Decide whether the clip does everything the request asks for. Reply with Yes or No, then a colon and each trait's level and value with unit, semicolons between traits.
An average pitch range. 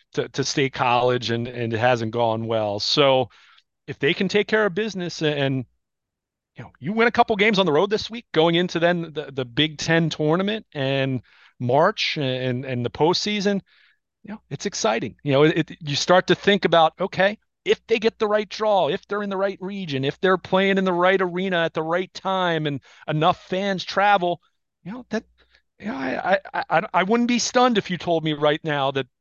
No: wide, 6.1 semitones